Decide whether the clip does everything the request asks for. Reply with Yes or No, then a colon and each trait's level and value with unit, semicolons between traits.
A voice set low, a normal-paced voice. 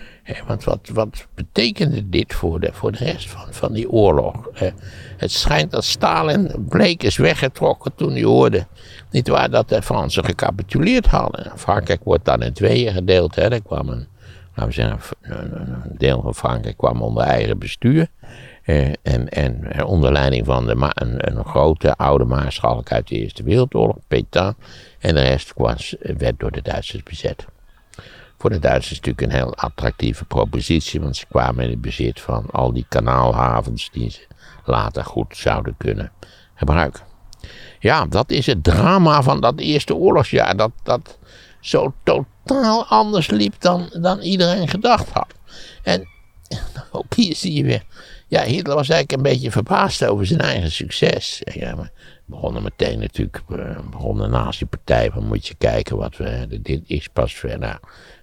Yes: very low, 95 Hz; average, 165 wpm